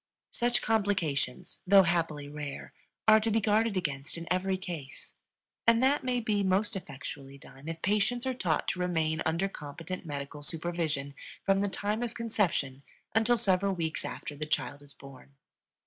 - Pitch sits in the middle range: Yes, medium, 180 Hz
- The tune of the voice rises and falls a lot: Yes, wide, 6.0 semitones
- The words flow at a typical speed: Yes, average, 165 wpm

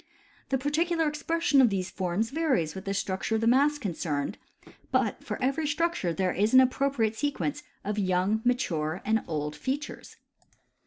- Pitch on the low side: No, high, 225 Hz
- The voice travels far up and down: Yes, wide, 7.5 semitones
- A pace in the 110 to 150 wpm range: No, average, 160 wpm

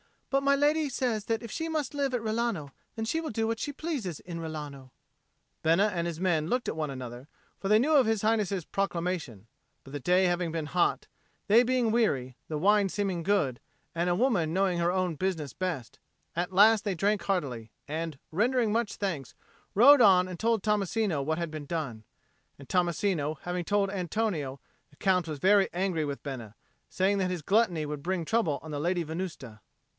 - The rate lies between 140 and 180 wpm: No, average, 190 wpm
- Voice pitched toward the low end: No, medium, 180 Hz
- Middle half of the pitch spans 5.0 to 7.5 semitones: Yes, wide, 5.6 semitones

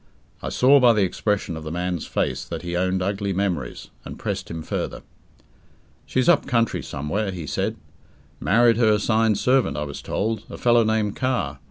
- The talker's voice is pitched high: No, low, 100 Hz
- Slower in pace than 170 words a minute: No, average, 180 wpm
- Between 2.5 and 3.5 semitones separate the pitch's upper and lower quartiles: No, average, 4.8 semitones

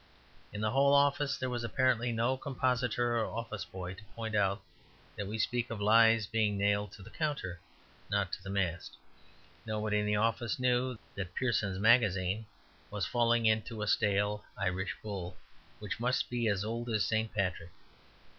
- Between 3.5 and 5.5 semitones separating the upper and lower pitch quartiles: No, average, 2.8 semitones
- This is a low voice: Yes, low, 110 Hz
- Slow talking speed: No, average, 175 wpm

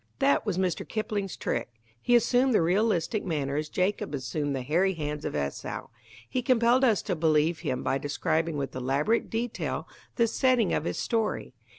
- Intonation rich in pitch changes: Yes, wide, 7.6 semitones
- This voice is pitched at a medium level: Yes, medium, 175 Hz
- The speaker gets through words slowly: No, average, 175 wpm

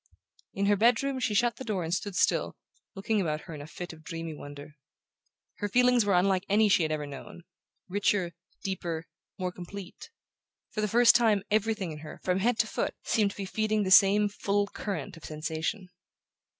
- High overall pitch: Yes, high, 195 Hz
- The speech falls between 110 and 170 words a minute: No, average, 190 wpm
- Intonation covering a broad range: No, average, 4.3 semitones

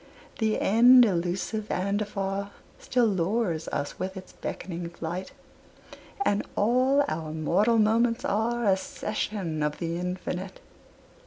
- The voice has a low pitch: No, high, 195 Hz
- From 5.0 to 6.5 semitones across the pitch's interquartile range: No, average, 4.0 semitones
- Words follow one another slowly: Yes, slow, 120 wpm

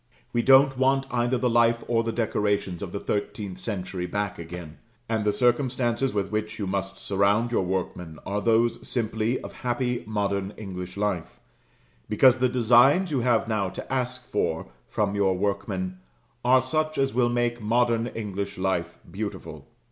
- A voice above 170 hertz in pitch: No, low, 110 Hz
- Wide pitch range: No, average, 3.7 semitones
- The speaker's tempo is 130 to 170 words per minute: Yes, average, 165 wpm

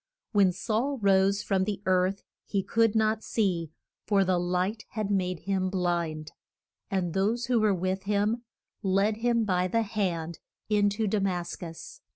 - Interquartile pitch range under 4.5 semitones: Yes, average, 2.8 semitones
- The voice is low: No, high, 195 Hz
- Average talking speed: Yes, average, 165 wpm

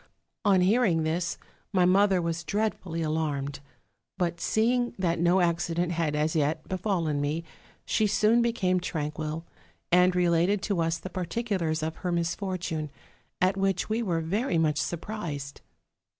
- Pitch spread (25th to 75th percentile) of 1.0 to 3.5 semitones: Yes, average, 3.2 semitones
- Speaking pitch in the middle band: Yes, medium, 175 Hz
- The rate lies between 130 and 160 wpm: Yes, average, 140 wpm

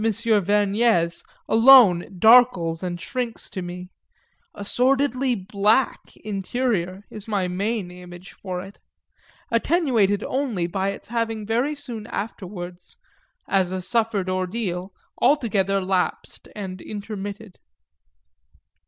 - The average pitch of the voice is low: No, high, 205 Hz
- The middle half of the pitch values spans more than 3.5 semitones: Yes, average, 3.9 semitones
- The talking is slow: Yes, slow, 105 wpm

